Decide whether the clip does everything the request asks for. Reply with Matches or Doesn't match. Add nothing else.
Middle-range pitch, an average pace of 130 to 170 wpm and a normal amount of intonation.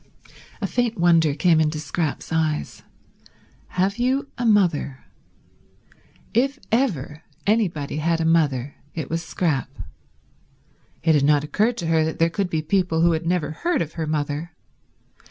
Matches